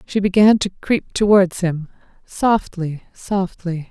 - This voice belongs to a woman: Yes, female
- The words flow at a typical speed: No, slow, 110 wpm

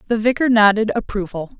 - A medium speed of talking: Yes, average, 150 wpm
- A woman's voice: Yes, female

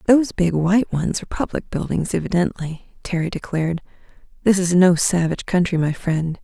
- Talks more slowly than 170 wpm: Yes, average, 160 wpm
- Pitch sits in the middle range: Yes, medium, 175 Hz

